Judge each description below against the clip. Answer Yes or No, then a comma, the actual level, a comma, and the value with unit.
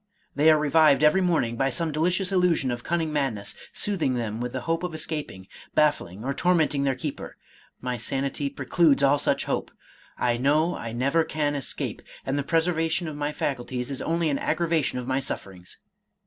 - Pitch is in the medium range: Yes, medium, 145 Hz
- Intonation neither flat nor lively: Yes, average, 3.9 semitones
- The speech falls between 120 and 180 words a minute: No, average, 190 wpm